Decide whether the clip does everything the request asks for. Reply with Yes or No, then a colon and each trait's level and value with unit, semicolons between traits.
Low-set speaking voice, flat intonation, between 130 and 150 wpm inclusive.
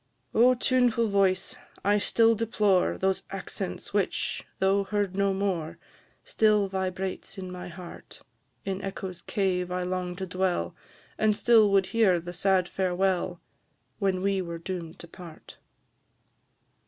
No: high, 190 Hz; narrow, 1.9 semitones; slow, 135 wpm